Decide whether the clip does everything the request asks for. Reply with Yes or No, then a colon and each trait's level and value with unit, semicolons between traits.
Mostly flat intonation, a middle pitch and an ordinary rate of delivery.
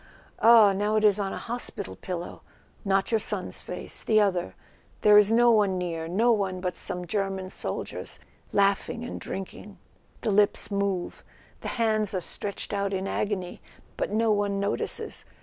No: narrow, 2.0 semitones; high, 200 Hz; average, 160 wpm